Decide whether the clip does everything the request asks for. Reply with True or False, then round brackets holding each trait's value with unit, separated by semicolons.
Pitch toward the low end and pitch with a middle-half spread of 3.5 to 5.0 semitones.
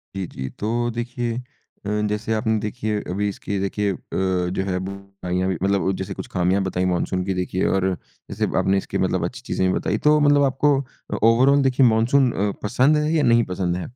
True (105 Hz; 4.2 semitones)